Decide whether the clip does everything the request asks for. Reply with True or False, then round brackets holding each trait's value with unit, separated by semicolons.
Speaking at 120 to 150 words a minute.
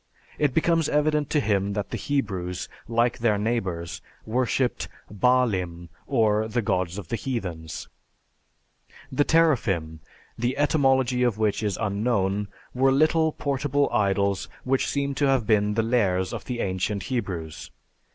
True (140 wpm)